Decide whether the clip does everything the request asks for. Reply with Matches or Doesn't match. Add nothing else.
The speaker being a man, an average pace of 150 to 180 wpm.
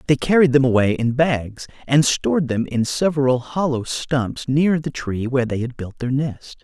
Doesn't match